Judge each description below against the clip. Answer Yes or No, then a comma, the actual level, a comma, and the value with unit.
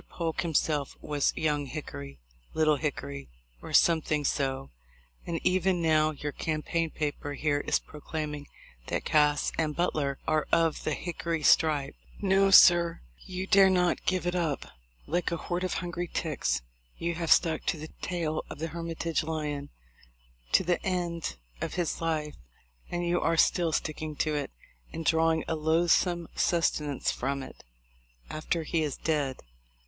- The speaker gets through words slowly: No, average, 155 wpm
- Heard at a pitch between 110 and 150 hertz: No, medium, 160 Hz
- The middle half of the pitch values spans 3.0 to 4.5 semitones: No, narrow, 2.5 semitones